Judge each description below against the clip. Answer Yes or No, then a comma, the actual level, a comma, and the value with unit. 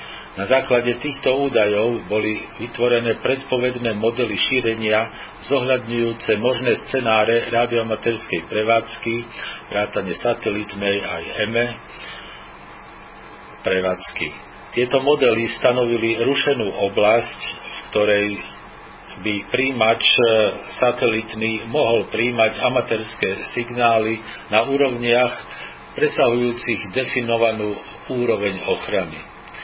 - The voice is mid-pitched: No, low, 115 Hz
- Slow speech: Yes, slow, 80 wpm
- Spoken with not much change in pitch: Yes, narrow, 1.9 semitones